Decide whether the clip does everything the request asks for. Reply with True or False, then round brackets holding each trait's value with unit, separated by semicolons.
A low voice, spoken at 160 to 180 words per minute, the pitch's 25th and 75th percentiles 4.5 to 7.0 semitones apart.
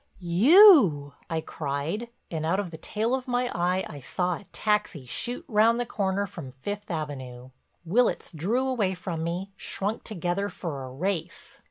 False (185 Hz; 165 wpm; 5.1 semitones)